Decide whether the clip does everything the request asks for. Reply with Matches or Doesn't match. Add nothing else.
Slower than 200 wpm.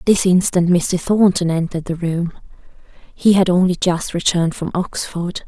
Matches